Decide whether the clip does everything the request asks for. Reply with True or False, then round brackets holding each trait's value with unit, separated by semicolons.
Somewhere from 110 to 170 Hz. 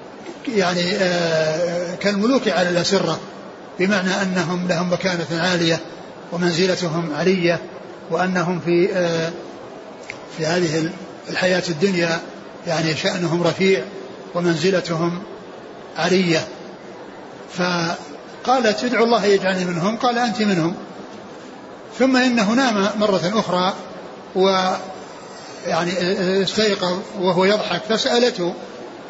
False (180 Hz)